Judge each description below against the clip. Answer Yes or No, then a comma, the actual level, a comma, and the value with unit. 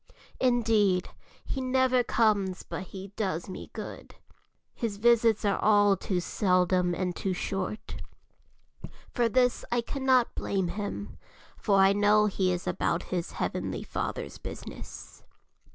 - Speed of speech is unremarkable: No, slow, 130 wpm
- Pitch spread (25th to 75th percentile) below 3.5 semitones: No, average, 3.9 semitones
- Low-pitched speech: No, high, 205 Hz